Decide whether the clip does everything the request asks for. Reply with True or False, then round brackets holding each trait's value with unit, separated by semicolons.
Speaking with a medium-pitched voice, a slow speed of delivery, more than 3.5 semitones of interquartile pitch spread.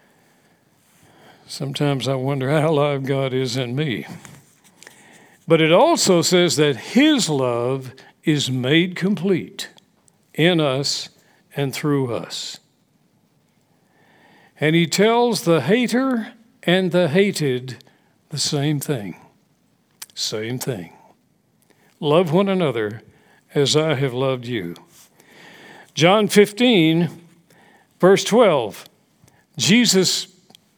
True (160 Hz; 95 wpm; 5.6 semitones)